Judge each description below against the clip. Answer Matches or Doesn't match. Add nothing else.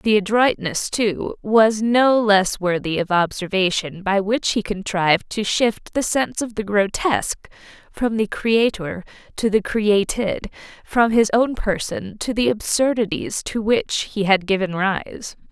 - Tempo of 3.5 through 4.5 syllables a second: Matches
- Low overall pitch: Doesn't match